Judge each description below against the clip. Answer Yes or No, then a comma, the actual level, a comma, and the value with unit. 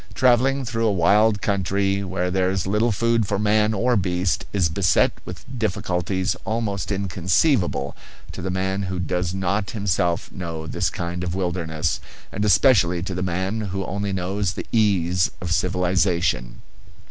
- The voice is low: Yes, very low, 95 Hz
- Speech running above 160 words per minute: No, average, 155 wpm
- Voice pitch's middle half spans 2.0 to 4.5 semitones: Yes, average, 2.7 semitones